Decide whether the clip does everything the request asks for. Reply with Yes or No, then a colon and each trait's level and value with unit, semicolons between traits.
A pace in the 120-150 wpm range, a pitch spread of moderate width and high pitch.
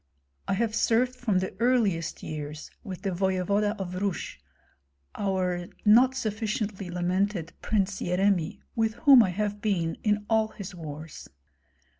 Yes: slow, 135 wpm; average, 3.3 semitones; high, 200 Hz